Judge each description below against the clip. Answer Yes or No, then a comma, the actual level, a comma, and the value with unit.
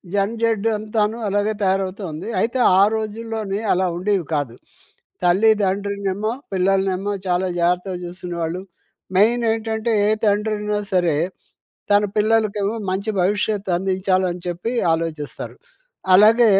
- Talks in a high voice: Yes, high, 200 Hz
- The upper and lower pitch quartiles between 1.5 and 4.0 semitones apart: Yes, average, 2.8 semitones